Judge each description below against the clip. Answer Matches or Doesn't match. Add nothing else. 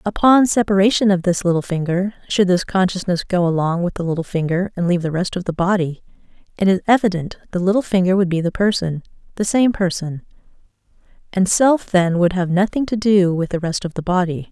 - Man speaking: Doesn't match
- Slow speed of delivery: Doesn't match